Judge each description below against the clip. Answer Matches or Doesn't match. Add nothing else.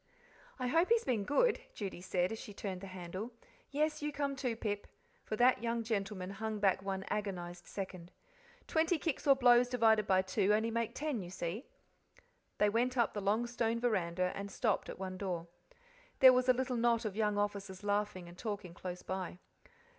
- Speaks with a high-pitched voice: Matches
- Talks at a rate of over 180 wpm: Matches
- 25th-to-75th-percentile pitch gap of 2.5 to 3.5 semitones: Doesn't match